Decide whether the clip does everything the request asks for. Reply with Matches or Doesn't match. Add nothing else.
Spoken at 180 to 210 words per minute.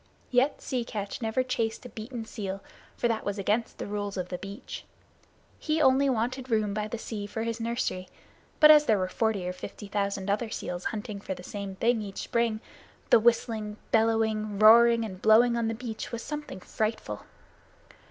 Matches